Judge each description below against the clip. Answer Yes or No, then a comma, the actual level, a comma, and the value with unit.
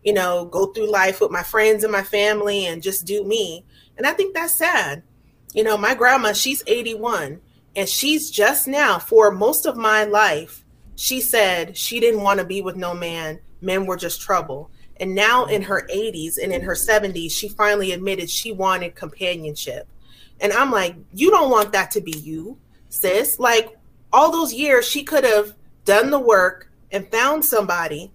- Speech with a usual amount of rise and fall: Yes, average, 4.4 semitones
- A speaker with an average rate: Yes, average, 190 wpm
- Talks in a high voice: Yes, high, 210 Hz